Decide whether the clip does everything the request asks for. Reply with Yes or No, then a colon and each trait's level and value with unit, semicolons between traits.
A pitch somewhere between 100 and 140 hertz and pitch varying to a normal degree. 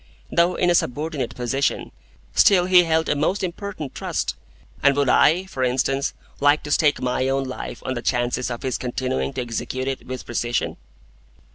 Yes: low, 135 Hz; average, 4.0 semitones